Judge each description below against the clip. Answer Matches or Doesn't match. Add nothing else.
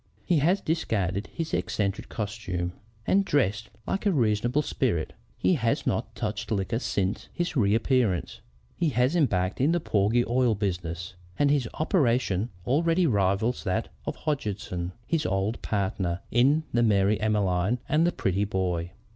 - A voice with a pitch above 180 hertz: Doesn't match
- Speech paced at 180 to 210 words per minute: Doesn't match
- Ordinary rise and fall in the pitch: Doesn't match